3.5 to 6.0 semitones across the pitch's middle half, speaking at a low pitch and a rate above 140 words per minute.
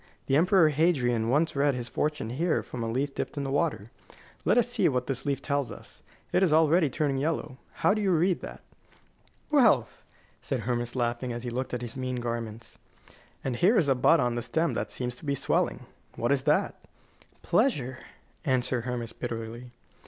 Yes: average, 4.1 semitones; low, 130 Hz; average, 190 wpm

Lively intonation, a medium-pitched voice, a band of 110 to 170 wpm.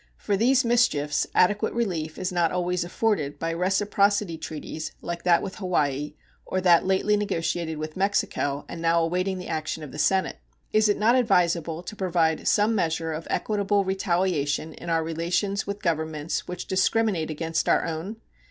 No: average, 3.8 semitones; medium, 175 Hz; average, 165 wpm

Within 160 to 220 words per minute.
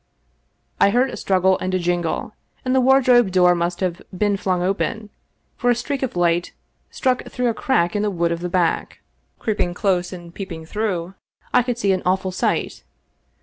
Yes: average, 190 wpm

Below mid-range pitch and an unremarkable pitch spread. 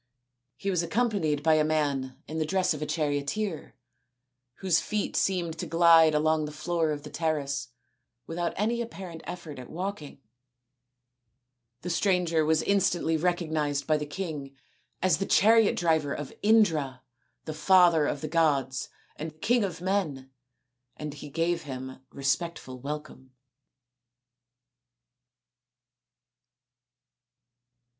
No: medium, 160 Hz; average, 3.3 semitones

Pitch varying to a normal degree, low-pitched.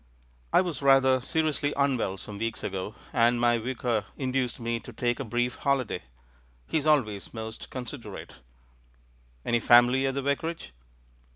Yes: average, 3.0 semitones; low, 125 Hz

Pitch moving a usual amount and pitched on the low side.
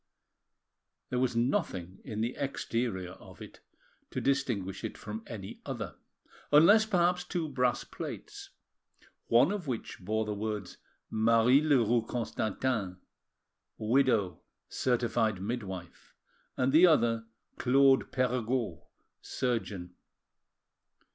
Yes: average, 4.0 semitones; low, 120 Hz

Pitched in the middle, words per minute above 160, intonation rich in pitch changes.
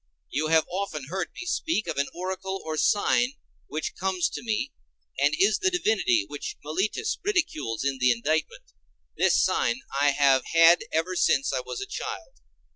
Yes: medium, 175 Hz; average, 170 wpm; wide, 9.0 semitones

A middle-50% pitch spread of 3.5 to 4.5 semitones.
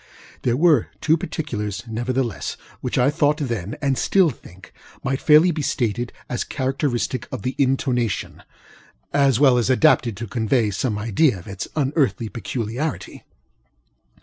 Yes: average, 4.2 semitones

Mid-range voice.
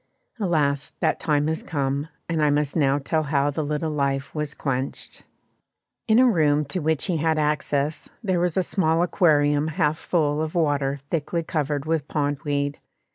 Yes: medium, 150 Hz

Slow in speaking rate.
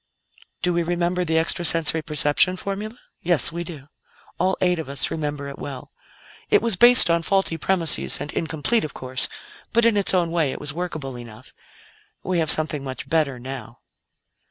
No: average, 180 wpm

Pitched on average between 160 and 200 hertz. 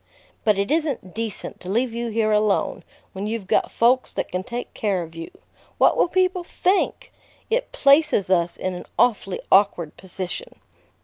No: high, 215 Hz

